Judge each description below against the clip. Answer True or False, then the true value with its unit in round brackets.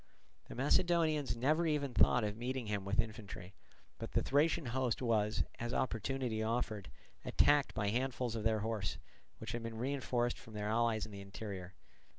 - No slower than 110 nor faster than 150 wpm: False (165 wpm)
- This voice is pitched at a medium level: False (115 Hz)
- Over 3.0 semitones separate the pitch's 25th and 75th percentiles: True (3.6 semitones)